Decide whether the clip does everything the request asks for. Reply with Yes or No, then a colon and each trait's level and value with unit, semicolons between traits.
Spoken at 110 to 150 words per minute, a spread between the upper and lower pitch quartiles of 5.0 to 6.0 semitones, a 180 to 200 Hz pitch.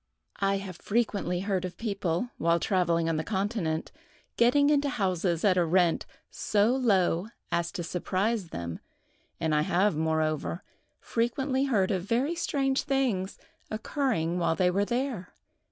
Yes: average, 145 wpm; wide, 5.5 semitones; high, 190 Hz